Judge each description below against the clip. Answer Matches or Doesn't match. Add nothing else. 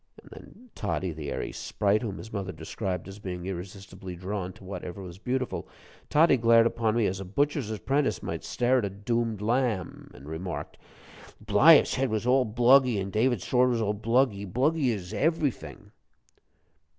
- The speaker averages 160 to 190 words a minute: Matches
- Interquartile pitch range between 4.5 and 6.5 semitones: Matches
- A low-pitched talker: Matches